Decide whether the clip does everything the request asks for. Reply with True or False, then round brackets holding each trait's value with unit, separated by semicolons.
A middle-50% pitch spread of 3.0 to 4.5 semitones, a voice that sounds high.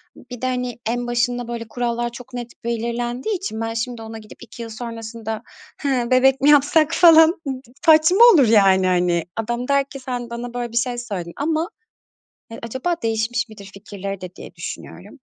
False (2.4 semitones; 240 Hz)